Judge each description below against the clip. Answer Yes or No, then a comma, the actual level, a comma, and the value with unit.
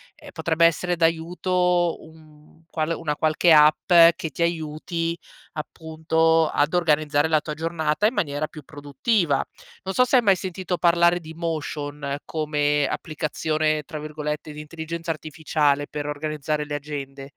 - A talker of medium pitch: Yes, medium, 155 Hz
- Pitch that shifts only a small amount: Yes, narrow, 2.0 semitones